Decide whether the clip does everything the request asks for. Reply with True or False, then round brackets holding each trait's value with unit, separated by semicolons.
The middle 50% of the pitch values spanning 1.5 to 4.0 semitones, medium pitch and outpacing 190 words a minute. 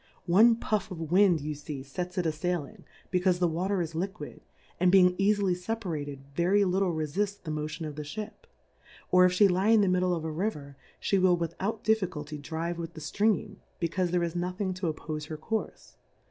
True (3.6 semitones; 180 Hz; 200 wpm)